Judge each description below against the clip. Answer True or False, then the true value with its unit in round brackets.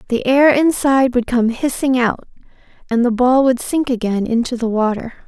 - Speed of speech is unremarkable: True (180 wpm)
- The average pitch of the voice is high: True (250 Hz)